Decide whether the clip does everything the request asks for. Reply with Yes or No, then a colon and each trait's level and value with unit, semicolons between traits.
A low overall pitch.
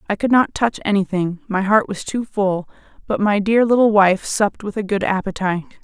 No: high, 205 Hz